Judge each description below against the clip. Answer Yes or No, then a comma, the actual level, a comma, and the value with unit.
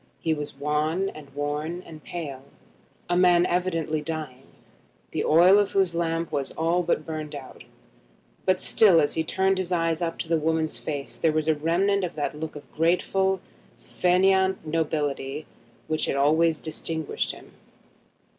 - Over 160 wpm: No, average, 155 wpm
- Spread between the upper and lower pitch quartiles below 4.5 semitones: Yes, average, 2.8 semitones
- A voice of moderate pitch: Yes, medium, 160 Hz